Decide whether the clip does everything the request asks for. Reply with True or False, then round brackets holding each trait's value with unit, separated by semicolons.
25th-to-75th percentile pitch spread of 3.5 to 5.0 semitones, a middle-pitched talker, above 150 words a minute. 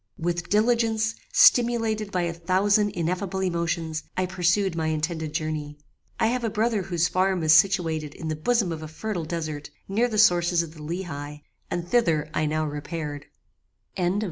True (4.6 semitones; 175 Hz; 165 wpm)